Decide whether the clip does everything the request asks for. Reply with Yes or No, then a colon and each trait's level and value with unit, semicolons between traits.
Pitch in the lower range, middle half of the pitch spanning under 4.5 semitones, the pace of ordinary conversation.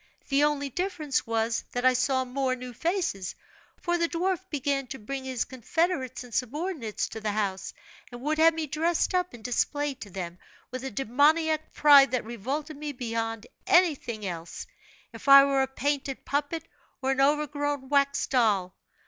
No: very high, 270 Hz; average, 3.8 semitones; average, 170 wpm